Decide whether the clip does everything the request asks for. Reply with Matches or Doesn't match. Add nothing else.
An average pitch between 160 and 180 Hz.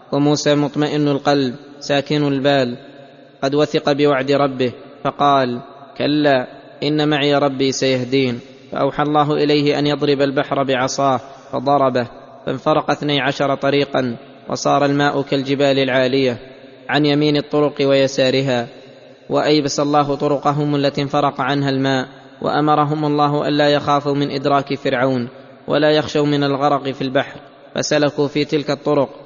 Doesn't match